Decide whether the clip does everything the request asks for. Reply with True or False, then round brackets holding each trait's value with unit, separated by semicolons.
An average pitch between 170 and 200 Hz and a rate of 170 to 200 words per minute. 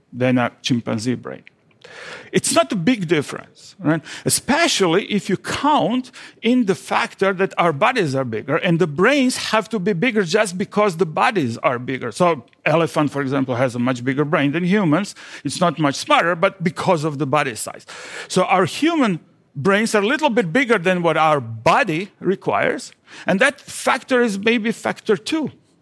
True (185 Hz; 180 wpm)